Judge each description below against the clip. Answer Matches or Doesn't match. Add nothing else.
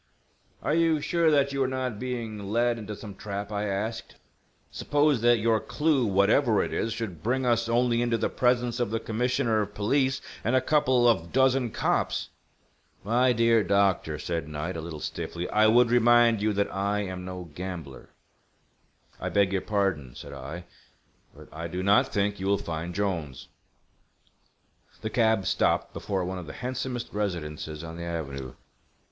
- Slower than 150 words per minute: Doesn't match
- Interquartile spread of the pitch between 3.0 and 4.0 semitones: Doesn't match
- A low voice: Matches